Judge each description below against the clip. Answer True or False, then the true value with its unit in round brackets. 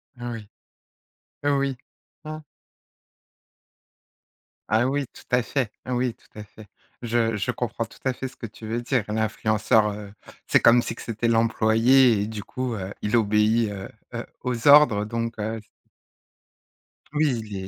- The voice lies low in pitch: True (115 Hz)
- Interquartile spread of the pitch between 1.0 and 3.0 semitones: True (2.7 semitones)